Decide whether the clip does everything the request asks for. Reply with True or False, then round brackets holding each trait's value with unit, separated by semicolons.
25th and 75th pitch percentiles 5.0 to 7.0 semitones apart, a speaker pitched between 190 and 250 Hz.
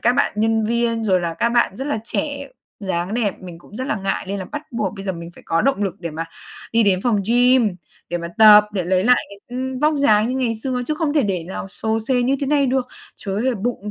False (4.6 semitones; 220 Hz)